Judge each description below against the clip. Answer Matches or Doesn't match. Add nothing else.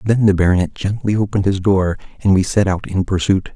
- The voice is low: Matches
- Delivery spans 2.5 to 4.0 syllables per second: Doesn't match